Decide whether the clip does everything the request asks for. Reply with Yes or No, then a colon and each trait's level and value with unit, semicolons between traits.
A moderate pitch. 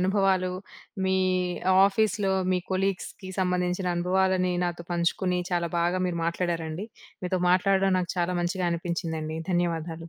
Yes: medium, 180 Hz